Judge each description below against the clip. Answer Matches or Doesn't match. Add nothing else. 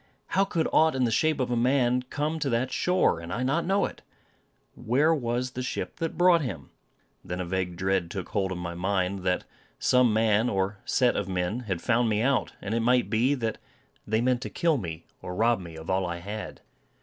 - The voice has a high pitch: Doesn't match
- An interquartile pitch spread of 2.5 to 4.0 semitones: Doesn't match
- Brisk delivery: Matches